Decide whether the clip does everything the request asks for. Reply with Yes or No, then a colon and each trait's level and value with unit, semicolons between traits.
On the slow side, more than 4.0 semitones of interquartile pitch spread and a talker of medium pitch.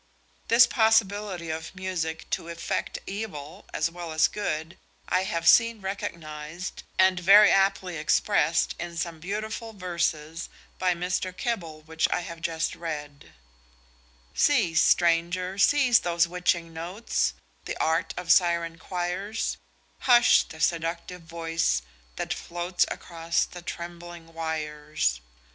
No: slow, 120 wpm; narrow, 2.5 semitones; medium, 170 Hz